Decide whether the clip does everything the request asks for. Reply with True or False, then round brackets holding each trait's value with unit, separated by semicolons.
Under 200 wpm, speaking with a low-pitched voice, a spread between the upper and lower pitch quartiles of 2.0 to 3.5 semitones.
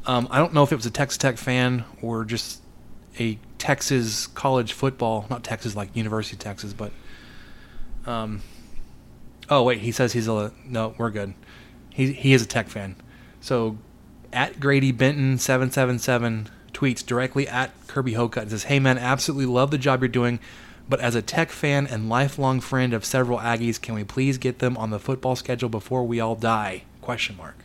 True (180 wpm; 120 Hz; 2.7 semitones)